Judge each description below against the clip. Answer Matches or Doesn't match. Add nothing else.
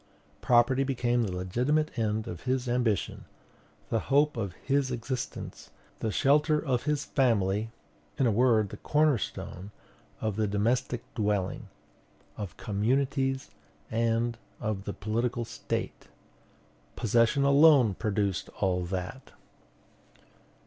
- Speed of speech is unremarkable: Doesn't match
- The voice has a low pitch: Matches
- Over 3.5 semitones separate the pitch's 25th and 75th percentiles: Matches